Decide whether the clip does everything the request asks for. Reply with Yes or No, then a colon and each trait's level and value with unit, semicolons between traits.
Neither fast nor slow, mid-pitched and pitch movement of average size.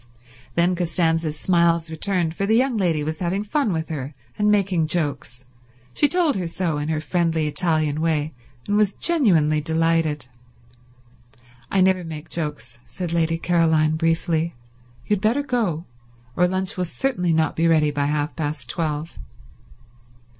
Yes: average, 155 wpm; medium, 165 Hz; average, 3.1 semitones